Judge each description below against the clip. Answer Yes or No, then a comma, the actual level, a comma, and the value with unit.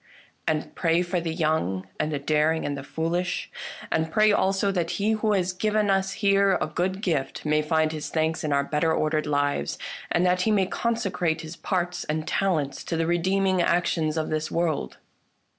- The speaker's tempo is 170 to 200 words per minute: Yes, average, 190 wpm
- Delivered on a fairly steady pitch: No, average, 3.5 semitones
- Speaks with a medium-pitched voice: Yes, medium, 165 Hz